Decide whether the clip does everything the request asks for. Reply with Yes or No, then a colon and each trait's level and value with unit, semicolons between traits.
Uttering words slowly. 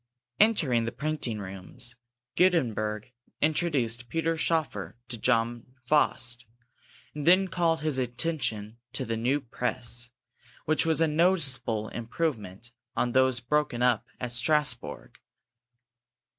Yes: slow, 115 wpm